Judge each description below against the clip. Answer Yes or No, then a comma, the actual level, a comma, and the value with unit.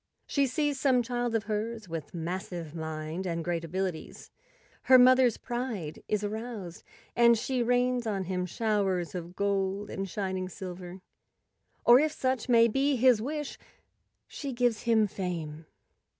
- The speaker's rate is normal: Yes, average, 150 wpm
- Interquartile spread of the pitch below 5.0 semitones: No, average, 5.3 semitones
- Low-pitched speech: No, high, 210 Hz